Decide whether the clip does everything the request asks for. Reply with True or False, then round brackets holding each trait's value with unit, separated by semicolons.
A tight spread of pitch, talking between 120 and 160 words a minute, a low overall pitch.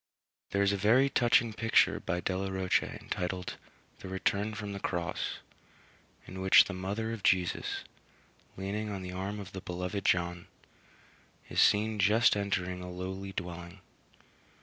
True (2.2 semitones; 145 wpm; 95 Hz)